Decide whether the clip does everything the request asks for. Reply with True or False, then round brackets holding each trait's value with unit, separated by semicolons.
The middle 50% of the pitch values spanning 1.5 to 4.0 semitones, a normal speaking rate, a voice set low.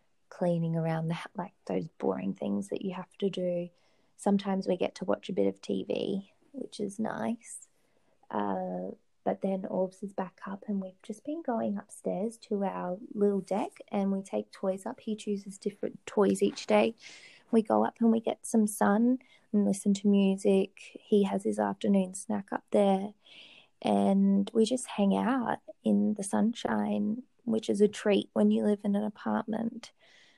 False (2.7 semitones; 175 wpm; 205 Hz)